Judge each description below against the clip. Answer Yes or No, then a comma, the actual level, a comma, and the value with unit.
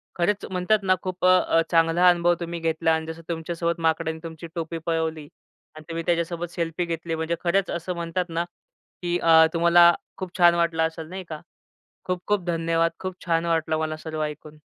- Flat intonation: Yes, narrow, 1.3 semitones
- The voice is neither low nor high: Yes, medium, 170 Hz